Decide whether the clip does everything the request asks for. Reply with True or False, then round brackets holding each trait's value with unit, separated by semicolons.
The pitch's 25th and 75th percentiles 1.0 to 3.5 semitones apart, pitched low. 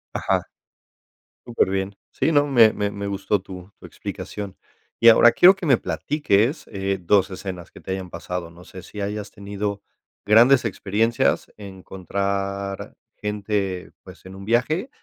True (2.9 semitones; 100 Hz)